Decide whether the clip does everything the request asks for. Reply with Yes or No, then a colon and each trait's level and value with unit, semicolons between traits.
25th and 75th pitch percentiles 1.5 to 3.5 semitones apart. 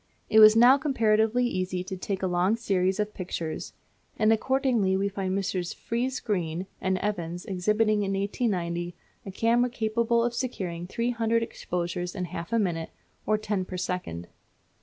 No: average, 4.0 semitones